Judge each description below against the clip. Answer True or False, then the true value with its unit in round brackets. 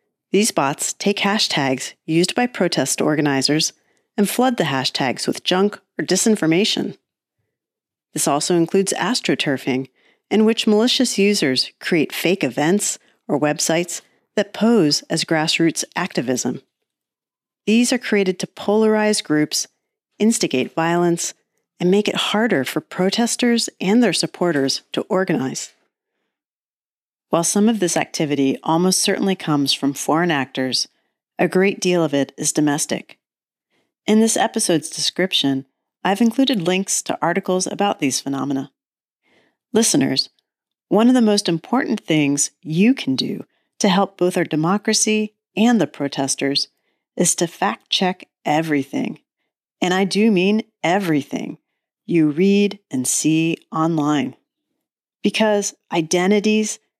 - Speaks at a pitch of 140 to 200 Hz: True (185 Hz)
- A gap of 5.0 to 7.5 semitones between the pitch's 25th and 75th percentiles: True (5.6 semitones)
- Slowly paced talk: True (125 wpm)